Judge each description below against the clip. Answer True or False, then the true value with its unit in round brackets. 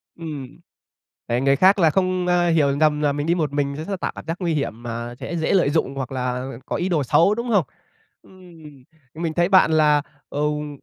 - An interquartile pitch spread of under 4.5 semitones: True (3.8 semitones)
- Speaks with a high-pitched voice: False (155 Hz)